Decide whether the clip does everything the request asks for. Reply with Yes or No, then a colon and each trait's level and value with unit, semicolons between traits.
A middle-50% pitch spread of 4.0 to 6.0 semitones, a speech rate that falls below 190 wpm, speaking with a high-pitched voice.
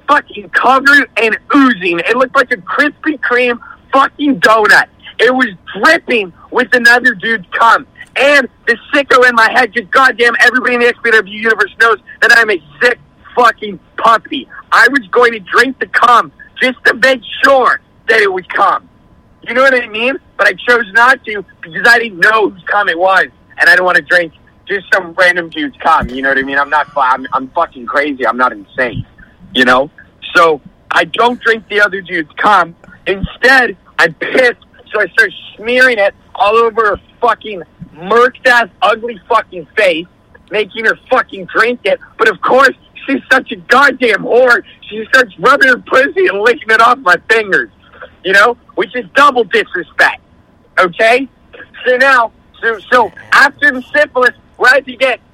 Yes: average, 5.0 semitones; average, 180 wpm; high, 240 Hz